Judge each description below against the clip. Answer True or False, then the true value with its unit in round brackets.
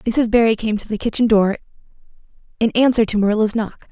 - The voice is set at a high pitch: True (220 Hz)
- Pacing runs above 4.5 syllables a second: True (6.3 syllables/s)